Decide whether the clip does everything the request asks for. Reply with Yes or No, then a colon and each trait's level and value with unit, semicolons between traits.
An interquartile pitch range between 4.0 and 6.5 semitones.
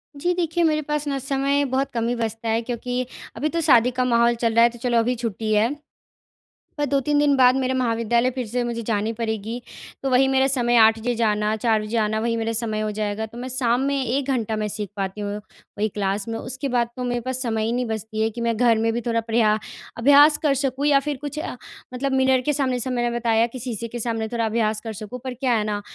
No: average, 2.9 semitones